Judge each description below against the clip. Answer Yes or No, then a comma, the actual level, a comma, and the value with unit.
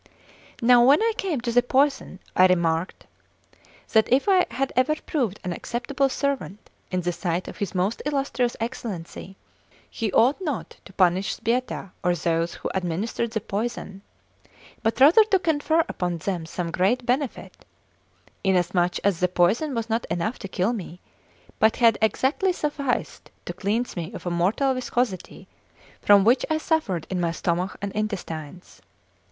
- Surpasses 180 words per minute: No, average, 160 wpm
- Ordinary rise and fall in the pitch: No, wide, 6.2 semitones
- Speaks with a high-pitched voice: Yes, high, 220 Hz